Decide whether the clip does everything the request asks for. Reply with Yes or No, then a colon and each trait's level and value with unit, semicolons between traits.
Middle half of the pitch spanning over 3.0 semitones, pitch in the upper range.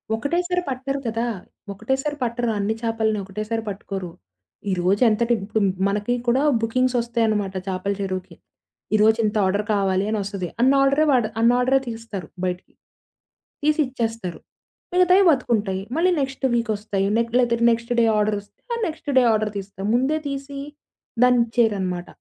Yes: average, 4.0 semitones; high, 225 Hz